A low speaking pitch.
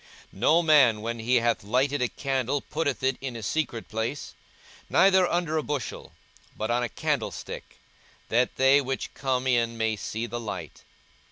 Yes: low, 125 Hz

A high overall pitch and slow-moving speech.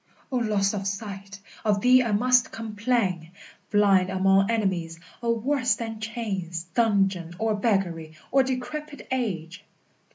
Yes: high, 205 Hz; slow, 130 wpm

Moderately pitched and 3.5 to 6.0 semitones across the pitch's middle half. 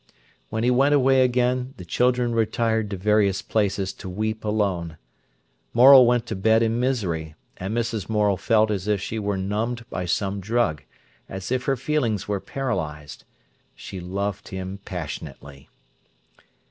No: low, 105 Hz; average, 4.2 semitones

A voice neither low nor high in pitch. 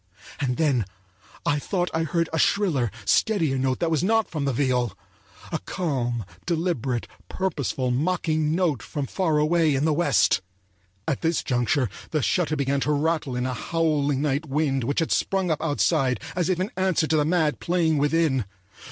Yes: medium, 150 Hz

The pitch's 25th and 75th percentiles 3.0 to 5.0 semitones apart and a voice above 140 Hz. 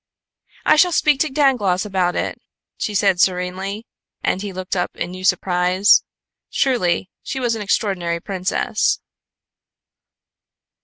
Yes: average, 3.6 semitones; high, 190 Hz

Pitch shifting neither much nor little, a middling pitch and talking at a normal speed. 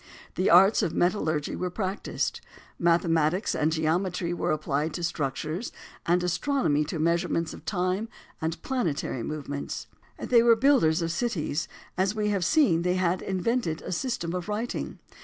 Yes: average, 4.0 semitones; medium, 175 Hz; average, 150 wpm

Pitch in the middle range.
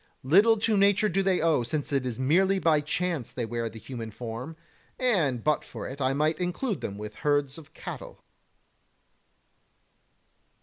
Yes: medium, 150 Hz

